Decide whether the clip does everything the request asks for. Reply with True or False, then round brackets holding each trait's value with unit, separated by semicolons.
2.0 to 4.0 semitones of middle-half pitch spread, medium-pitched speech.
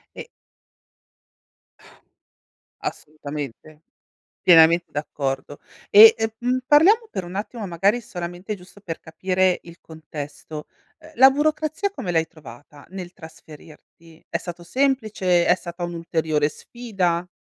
False (5.3 semitones; 175 Hz)